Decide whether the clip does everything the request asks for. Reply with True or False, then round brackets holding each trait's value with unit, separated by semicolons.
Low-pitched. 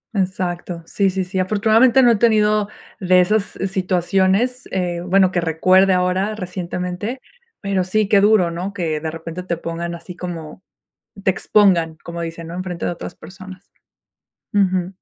False (185 Hz)